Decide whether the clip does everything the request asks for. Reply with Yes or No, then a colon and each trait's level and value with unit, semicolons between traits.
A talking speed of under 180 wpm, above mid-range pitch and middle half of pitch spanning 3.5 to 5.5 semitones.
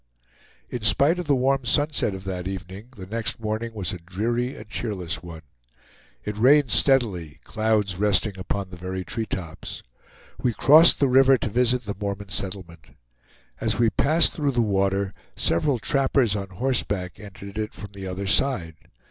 No: average, 165 wpm; low, 105 Hz; average, 4.7 semitones